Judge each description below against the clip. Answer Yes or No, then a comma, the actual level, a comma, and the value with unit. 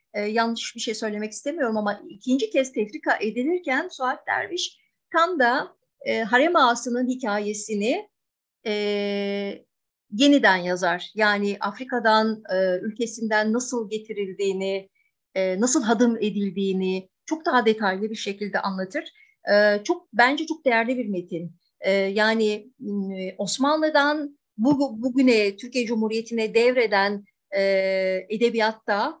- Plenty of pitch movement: No, average, 4.2 semitones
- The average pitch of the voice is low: No, high, 220 Hz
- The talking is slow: No, average, 115 wpm